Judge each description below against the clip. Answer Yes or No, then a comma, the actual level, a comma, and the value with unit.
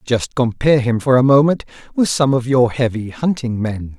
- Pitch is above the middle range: No, low, 125 Hz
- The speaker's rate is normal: Yes, average, 195 wpm